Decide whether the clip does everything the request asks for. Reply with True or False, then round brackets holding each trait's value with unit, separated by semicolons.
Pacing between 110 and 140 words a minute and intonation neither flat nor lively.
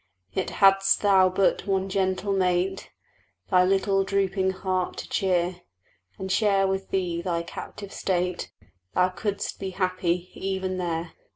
False (135 wpm; 1.1 semitones)